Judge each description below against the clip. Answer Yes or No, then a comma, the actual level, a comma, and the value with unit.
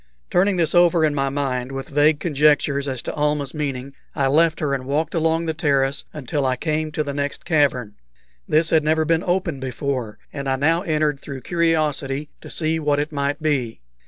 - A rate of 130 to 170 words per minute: No, average, 195 wpm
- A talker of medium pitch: Yes, medium, 150 Hz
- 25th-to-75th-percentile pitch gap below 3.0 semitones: Yes, narrow, 2.5 semitones